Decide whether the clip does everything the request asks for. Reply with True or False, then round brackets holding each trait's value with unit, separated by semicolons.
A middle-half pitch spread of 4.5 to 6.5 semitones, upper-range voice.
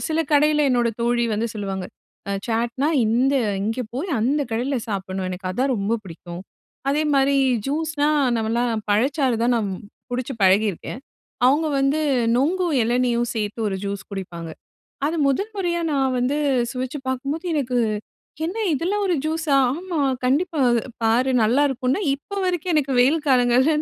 True (4.8 semitones; 255 Hz)